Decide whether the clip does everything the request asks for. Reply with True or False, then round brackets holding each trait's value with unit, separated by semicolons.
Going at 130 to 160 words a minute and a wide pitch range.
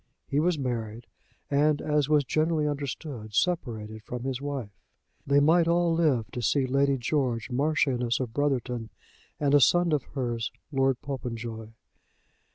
False (145 wpm; 3.8 semitones)